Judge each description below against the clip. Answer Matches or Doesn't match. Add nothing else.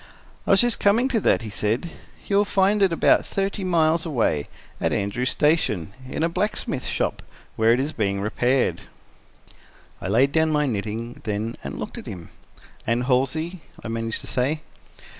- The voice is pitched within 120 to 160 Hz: Matches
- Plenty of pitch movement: Matches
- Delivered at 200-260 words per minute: Doesn't match